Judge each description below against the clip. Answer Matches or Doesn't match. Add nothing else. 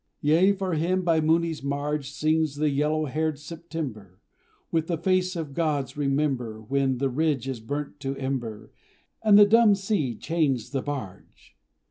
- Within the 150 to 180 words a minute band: Matches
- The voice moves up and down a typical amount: Matches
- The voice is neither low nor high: Matches